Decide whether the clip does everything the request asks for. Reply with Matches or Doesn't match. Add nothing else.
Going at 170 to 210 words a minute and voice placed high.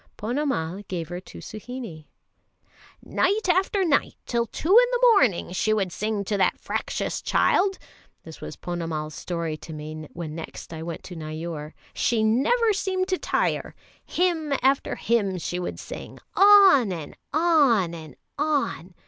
Doesn't match